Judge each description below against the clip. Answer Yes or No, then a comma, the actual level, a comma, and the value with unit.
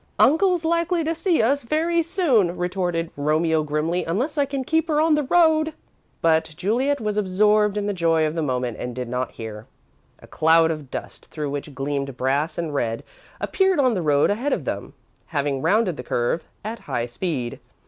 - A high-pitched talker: No, medium, 175 Hz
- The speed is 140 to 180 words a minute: No, average, 190 wpm